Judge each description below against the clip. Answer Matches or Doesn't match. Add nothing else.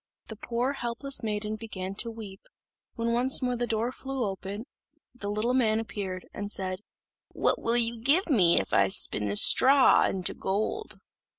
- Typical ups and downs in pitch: Matches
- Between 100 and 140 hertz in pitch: Doesn't match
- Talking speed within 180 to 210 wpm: Doesn't match